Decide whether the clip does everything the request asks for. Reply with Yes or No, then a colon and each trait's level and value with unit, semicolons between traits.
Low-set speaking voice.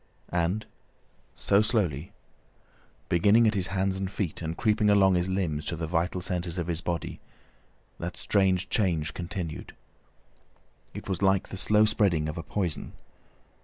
Yes: very low, 95 Hz